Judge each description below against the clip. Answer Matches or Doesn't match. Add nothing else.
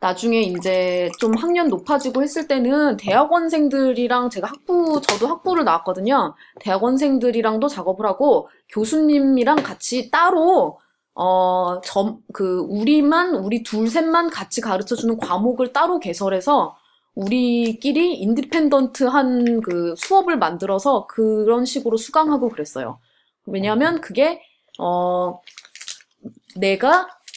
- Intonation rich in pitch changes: Matches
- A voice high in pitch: Matches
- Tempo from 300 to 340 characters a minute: Doesn't match